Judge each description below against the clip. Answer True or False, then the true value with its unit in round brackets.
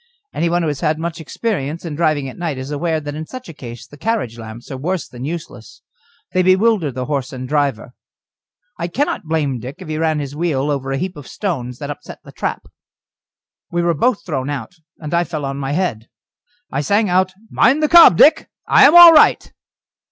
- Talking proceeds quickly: True (210 wpm)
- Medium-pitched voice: True (155 Hz)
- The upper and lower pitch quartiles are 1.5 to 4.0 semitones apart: False (4.6 semitones)